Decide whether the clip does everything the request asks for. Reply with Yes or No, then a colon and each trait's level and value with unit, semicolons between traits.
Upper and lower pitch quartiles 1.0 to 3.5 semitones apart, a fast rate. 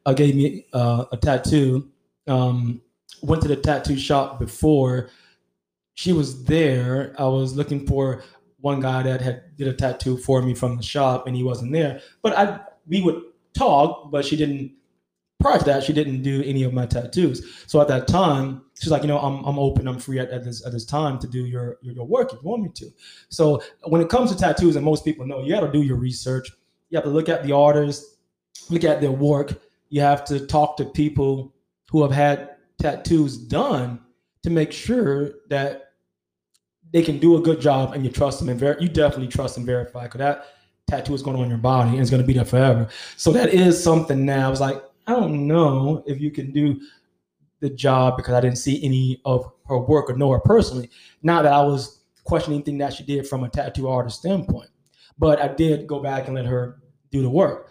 Yes: average, 2.7 semitones; fast, 220 wpm